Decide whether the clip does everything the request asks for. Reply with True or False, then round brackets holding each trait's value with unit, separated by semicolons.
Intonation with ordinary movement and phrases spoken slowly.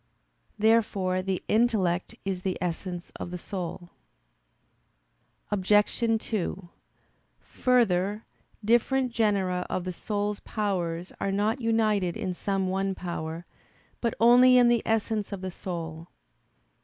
True (3.6 semitones; 120 wpm)